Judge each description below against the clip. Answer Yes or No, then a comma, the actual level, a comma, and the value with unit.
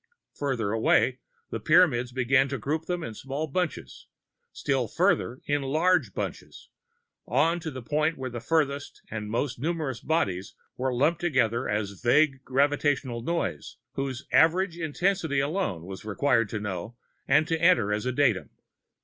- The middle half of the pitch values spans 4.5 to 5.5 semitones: Yes, average, 5.1 semitones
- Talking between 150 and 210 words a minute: Yes, average, 160 wpm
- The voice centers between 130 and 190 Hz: Yes, low, 135 Hz